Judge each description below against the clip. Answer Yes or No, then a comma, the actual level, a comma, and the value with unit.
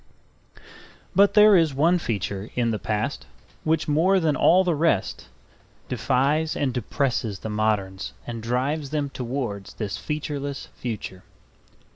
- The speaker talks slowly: Yes, slow, 130 wpm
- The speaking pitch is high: No, low, 135 Hz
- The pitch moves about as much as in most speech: No, wide, 6.2 semitones